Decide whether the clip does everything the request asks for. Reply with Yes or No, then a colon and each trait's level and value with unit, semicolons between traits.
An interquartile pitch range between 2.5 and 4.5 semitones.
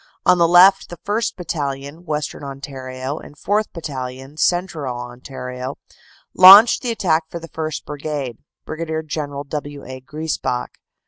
Yes: average, 4.0 semitones